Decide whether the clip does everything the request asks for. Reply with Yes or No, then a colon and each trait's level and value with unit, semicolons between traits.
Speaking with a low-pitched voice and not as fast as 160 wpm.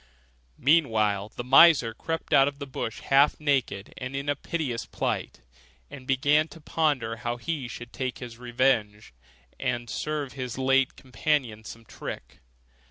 Yes: low, 130 Hz; average, 150 wpm